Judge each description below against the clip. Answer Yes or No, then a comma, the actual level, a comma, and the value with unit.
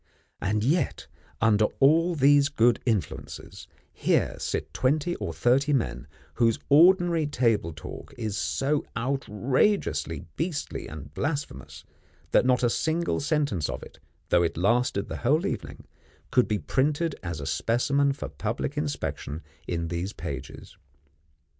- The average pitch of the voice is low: Yes, low, 125 Hz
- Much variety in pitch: Yes, wide, 6.3 semitones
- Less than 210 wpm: Yes, slow, 135 wpm